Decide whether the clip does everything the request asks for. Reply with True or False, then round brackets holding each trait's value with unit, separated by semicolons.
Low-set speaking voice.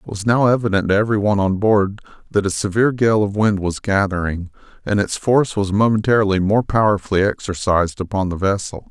True (100 Hz)